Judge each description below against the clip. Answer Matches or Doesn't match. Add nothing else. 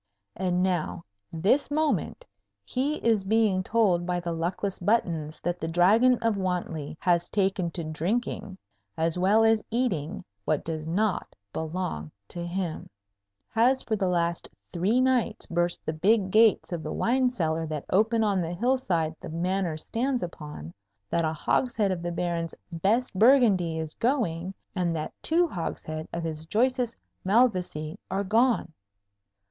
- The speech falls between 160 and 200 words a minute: Doesn't match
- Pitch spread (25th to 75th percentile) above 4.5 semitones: Matches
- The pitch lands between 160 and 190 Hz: Matches